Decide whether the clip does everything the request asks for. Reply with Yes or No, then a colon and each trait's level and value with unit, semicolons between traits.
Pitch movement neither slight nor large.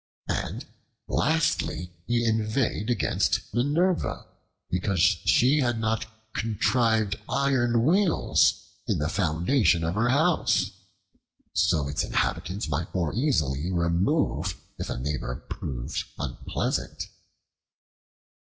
No: wide, 7.0 semitones